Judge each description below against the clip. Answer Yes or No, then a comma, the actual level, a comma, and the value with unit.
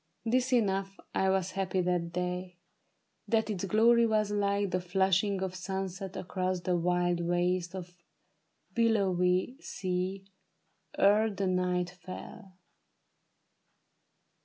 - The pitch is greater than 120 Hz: Yes, medium, 185 Hz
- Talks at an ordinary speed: No, slow, 115 wpm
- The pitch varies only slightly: Yes, narrow, 1.9 semitones